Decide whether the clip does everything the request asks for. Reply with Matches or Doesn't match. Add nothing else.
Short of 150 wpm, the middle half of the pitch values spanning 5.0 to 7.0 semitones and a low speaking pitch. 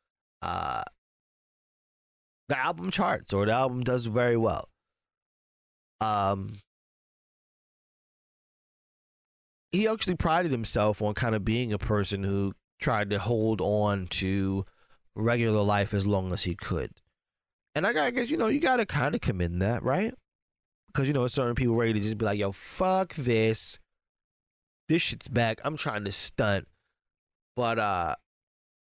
Doesn't match